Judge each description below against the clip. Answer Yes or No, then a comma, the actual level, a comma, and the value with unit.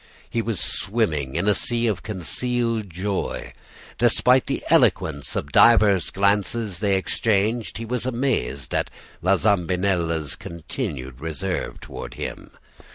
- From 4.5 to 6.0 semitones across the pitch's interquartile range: Yes, average, 5.3 semitones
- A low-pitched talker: Yes, low, 100 Hz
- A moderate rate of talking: No, slow, 125 wpm